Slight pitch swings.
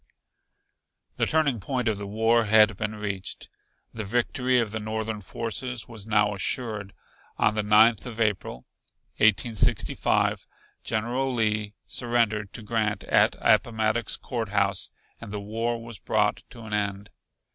Yes: narrow, 1.9 semitones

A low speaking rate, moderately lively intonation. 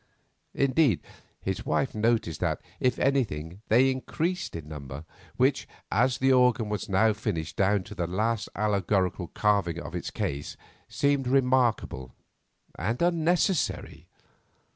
No: slow, 125 wpm; wide, 6.2 semitones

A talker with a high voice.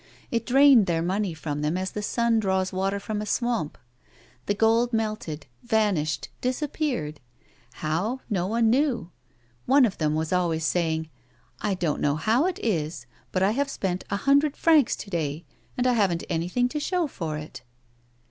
Yes: high, 200 Hz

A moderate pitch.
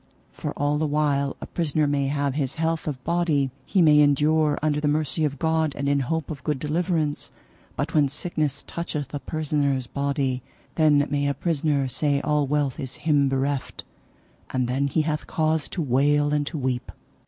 Yes: medium, 145 Hz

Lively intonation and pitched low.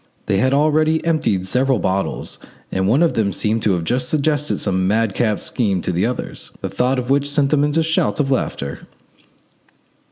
Yes: wide, 6.7 semitones; low, 125 Hz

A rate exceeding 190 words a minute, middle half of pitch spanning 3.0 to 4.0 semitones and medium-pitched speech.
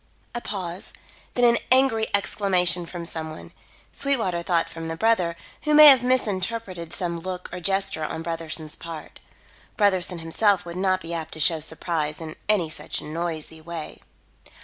No: average, 160 wpm; average, 3.6 semitones; medium, 175 Hz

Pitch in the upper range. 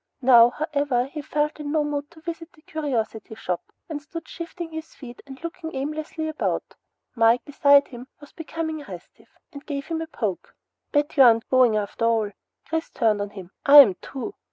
Yes: very high, 285 Hz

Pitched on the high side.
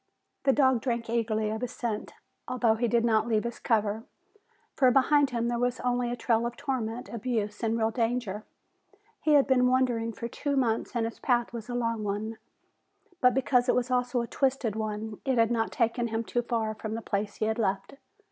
Yes: high, 235 Hz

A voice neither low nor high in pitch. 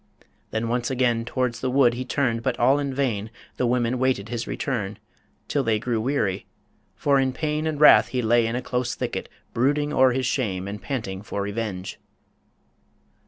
No: low, 120 Hz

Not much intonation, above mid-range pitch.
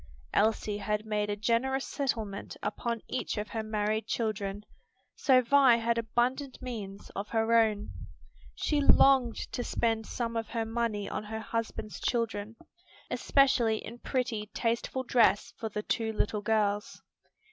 Yes: narrow, 2.1 semitones; high, 225 Hz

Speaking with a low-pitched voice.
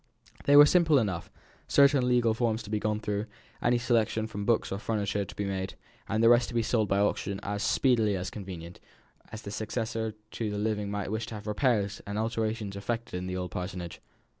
Yes: low, 110 Hz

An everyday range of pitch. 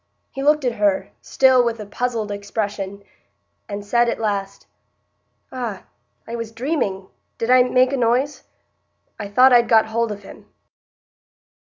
Yes: average, 3.6 semitones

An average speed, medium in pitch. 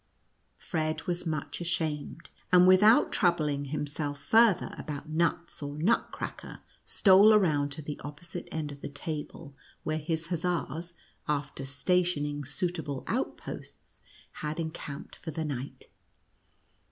No: slow, 130 wpm; medium, 155 Hz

